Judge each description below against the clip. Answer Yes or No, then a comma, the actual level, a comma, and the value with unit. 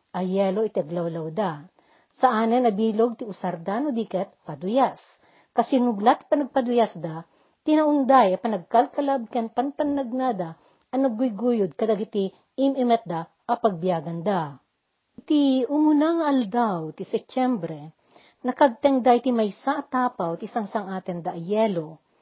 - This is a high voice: Yes, high, 230 Hz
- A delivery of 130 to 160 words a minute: No, slow, 110 wpm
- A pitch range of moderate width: No, wide, 5.7 semitones